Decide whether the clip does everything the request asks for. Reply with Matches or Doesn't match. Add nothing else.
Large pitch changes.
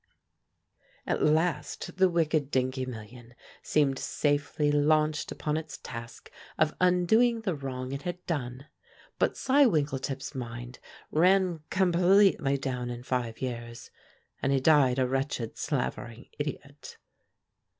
Doesn't match